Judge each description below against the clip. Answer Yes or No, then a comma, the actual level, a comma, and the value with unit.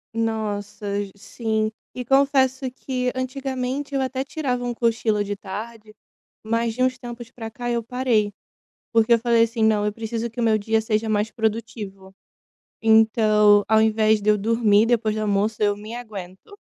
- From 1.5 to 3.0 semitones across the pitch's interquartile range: Yes, narrow, 2.4 semitones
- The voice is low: No, high, 225 Hz